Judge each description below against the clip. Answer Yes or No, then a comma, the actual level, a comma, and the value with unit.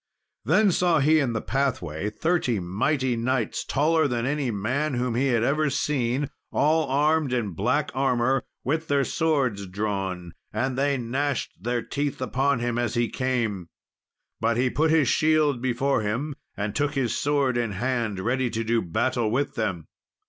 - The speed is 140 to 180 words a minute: Yes, average, 165 wpm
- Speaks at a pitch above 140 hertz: No, low, 130 Hz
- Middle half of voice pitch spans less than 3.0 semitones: No, average, 3.8 semitones